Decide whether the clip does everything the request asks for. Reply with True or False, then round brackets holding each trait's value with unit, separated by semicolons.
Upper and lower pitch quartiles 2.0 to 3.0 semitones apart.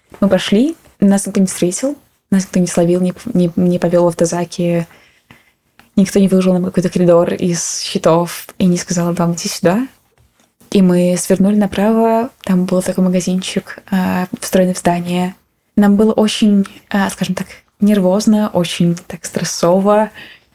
True (2.5 semitones)